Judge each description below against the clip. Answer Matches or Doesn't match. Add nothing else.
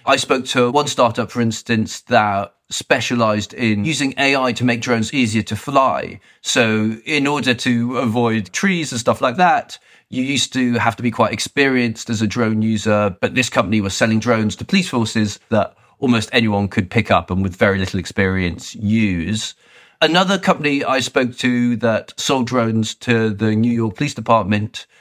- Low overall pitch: Matches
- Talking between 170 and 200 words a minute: Matches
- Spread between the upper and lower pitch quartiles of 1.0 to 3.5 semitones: Matches